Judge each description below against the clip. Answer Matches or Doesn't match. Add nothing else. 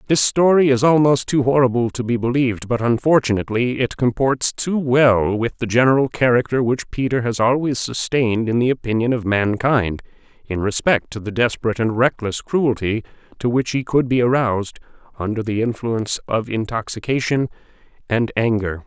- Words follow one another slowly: Doesn't match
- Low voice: Matches